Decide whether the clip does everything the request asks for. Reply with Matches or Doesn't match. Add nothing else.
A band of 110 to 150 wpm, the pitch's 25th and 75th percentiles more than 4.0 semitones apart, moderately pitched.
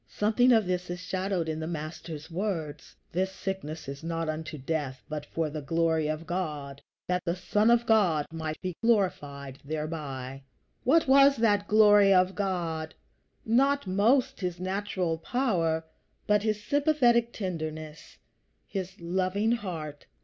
Matches